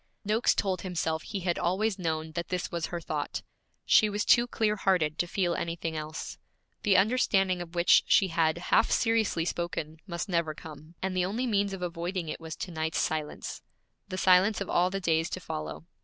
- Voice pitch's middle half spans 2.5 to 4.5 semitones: Yes, average, 3.1 semitones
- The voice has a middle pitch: Yes, medium, 180 Hz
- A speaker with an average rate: Yes, average, 195 wpm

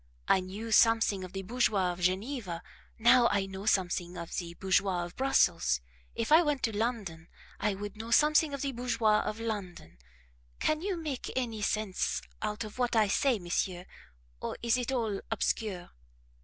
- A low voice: No, high, 215 Hz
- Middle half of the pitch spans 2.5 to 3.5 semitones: No, average, 4.5 semitones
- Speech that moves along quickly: No, average, 170 wpm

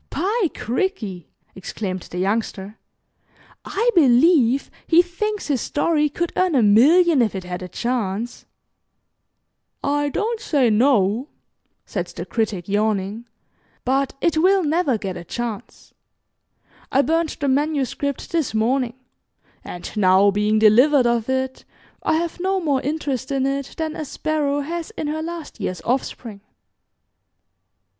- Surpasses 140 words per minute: No, slow, 135 wpm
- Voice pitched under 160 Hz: No, very high, 265 Hz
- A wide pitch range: Yes, wide, 6.5 semitones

